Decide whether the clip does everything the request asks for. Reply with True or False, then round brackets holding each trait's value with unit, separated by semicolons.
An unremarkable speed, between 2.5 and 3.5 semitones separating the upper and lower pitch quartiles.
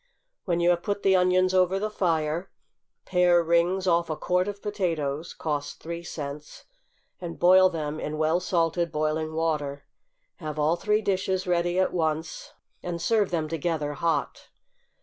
True (155 wpm; 2.8 semitones)